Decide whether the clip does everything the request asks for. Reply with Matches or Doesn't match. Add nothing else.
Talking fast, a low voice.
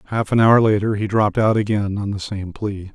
Matches